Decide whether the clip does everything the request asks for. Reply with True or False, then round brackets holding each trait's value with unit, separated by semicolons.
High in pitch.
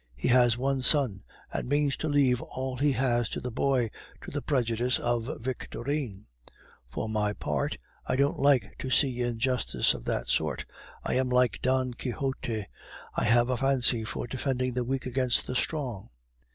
False (125 Hz)